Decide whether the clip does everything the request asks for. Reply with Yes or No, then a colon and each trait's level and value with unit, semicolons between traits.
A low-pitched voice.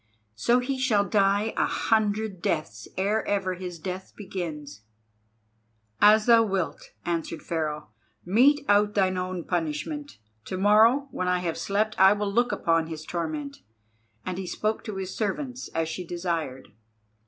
No: high, 190 Hz